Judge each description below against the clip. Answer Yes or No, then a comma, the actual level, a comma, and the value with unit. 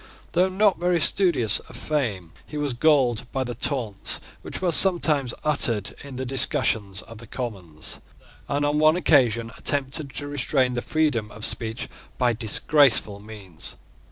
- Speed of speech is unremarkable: Yes, average, 155 wpm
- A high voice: No, low, 130 Hz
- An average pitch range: Yes, average, 5.0 semitones